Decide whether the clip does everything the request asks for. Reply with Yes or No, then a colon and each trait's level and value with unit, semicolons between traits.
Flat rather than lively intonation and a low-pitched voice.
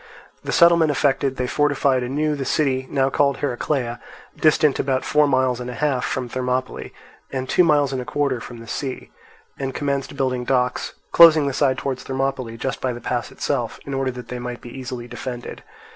Yes: narrow, 2.1 semitones; low, 130 Hz